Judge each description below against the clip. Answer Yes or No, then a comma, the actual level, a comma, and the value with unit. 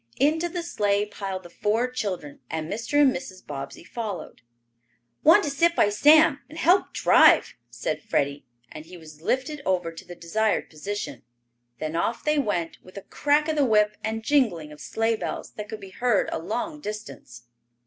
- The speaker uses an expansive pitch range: Yes, wide, 8.0 semitones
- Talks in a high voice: Yes, high, 210 Hz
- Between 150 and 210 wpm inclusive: Yes, average, 180 wpm